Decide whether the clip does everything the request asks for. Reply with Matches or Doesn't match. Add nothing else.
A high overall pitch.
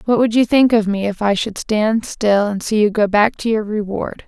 Matches